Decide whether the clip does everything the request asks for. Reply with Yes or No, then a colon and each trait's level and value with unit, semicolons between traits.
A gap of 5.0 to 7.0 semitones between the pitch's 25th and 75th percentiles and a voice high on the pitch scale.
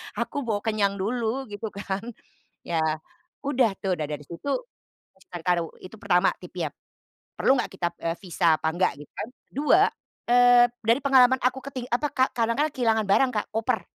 Yes: average, 5.3 semitones; high, 225 Hz